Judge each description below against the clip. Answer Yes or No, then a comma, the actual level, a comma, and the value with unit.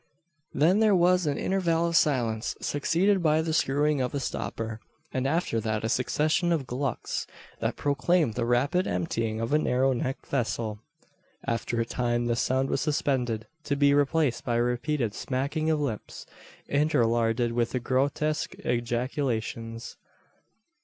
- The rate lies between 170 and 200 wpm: No, average, 145 wpm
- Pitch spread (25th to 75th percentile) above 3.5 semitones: Yes, average, 4.4 semitones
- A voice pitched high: No, low, 130 Hz